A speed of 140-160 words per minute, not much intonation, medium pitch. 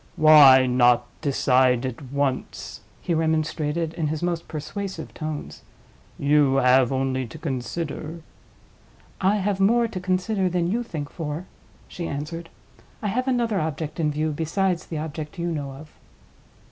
No: average, 145 wpm; average, 3.9 semitones; medium, 155 Hz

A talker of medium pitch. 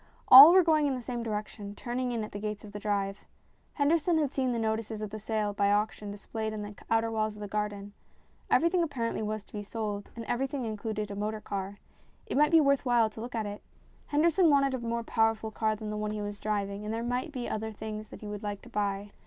No: high, 220 Hz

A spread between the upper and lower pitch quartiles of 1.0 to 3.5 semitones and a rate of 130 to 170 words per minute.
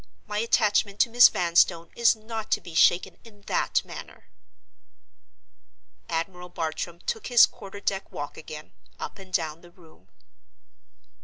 No: average, 4.3 semitones; average, 140 wpm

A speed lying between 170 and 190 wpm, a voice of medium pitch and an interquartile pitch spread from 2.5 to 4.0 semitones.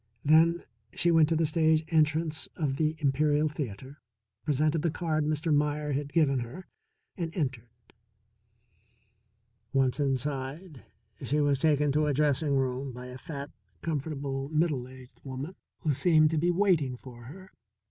No: average, 145 wpm; medium, 150 Hz; average, 2.8 semitones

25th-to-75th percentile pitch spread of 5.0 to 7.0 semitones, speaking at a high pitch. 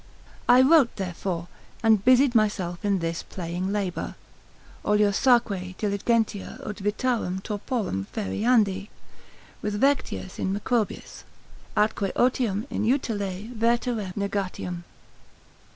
No: average, 3.7 semitones; high, 205 Hz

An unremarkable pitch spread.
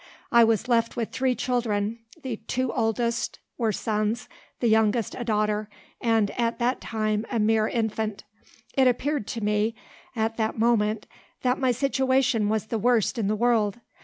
No: narrow, 2.1 semitones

